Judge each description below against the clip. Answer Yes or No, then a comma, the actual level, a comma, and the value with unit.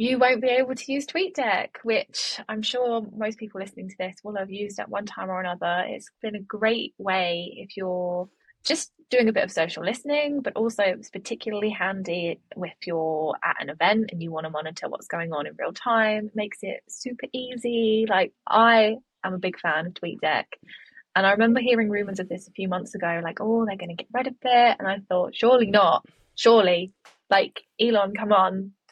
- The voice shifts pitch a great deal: No, average, 4.0 semitones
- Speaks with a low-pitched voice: No, high, 210 Hz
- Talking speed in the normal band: No, fast, 210 wpm